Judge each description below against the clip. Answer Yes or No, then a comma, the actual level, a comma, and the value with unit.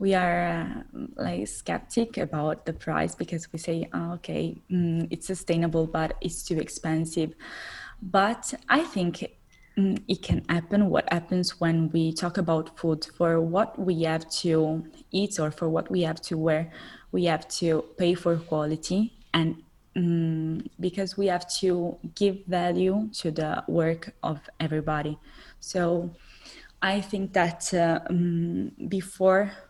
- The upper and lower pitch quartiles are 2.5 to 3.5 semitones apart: Yes, average, 2.9 semitones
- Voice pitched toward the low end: No, medium, 175 Hz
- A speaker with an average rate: Yes, average, 145 wpm